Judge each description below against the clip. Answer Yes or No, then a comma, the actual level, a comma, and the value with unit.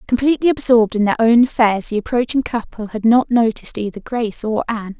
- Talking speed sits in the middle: Yes, average, 190 wpm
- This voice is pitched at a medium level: No, high, 230 Hz